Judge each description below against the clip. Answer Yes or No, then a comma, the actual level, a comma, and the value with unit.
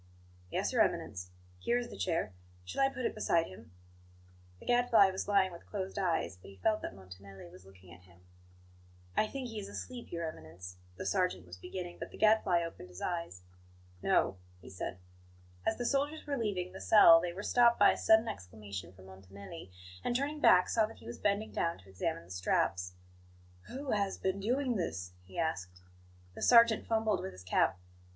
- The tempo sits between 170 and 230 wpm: Yes, average, 195 wpm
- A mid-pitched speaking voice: Yes, medium, 170 Hz